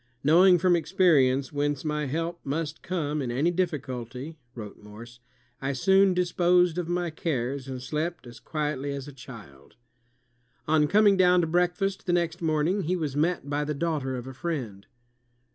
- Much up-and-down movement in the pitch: No, average, 4.7 semitones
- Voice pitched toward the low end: No, medium, 150 Hz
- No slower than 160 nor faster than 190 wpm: Yes, average, 165 wpm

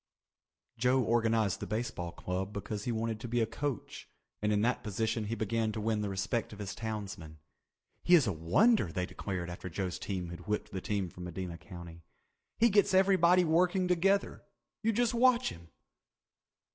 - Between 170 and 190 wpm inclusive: Yes, average, 180 wpm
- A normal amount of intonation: No, wide, 7.6 semitones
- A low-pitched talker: Yes, low, 110 Hz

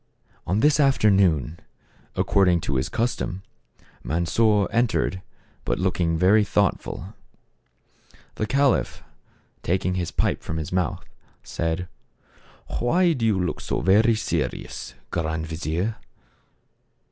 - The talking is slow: Yes, slow, 110 wpm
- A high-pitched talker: No, very low, 95 Hz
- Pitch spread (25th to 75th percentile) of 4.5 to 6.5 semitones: Yes, average, 5.0 semitones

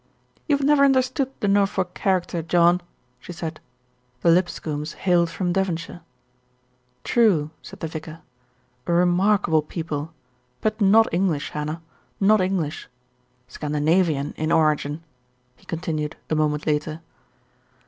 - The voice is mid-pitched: Yes, medium, 170 Hz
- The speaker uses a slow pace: Yes, slow, 125 wpm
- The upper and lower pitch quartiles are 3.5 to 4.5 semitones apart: Yes, average, 3.8 semitones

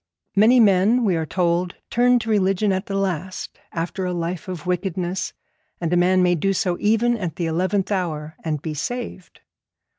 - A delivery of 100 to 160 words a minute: No, average, 180 wpm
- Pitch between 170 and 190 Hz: Yes, medium, 185 Hz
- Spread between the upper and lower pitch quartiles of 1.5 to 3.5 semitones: Yes, average, 2.8 semitones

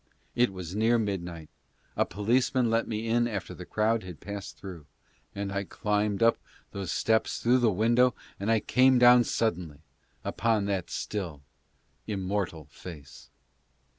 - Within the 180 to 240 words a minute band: No, average, 150 wpm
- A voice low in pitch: Yes, low, 105 Hz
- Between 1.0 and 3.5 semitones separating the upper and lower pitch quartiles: No, average, 3.9 semitones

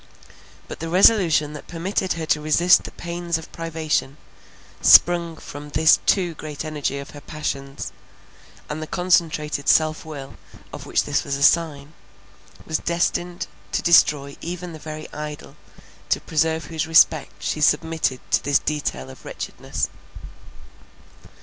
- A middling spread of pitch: No, narrow, 2.1 semitones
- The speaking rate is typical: Yes, average, 145 wpm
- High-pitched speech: No, medium, 155 Hz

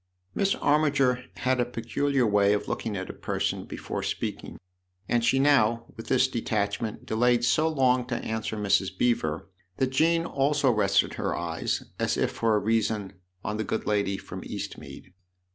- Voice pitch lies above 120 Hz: No, low, 115 Hz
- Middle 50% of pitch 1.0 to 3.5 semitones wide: No, average, 4.0 semitones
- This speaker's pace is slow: No, average, 165 wpm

